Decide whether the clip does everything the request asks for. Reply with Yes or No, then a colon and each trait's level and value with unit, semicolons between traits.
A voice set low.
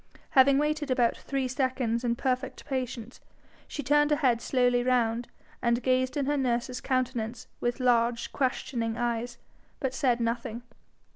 No: very high, 250 Hz